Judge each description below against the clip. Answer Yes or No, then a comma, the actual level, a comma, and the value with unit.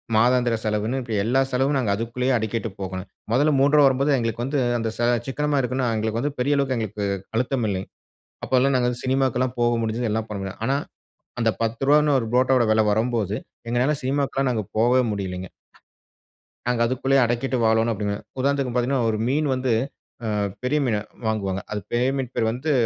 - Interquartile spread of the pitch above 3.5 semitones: No, average, 3.2 semitones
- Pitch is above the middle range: No, low, 120 Hz